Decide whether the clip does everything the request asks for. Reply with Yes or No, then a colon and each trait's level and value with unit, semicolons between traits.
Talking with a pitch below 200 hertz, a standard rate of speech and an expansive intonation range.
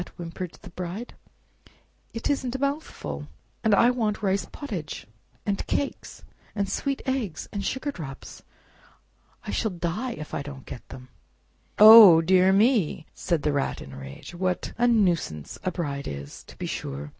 Yes: medium, 185 Hz; average, 160 wpm; wide, 7.4 semitones